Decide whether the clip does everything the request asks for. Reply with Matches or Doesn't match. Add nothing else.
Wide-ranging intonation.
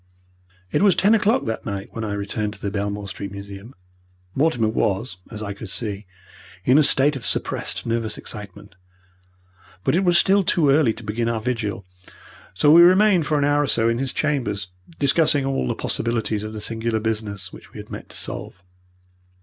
Matches